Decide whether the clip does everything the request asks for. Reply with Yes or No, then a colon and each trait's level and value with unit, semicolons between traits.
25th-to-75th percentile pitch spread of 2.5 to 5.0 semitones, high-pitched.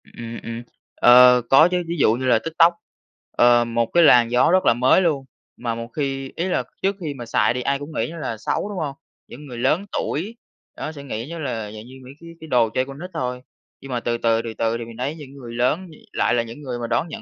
No: average, 4.7 semitones; low, 130 Hz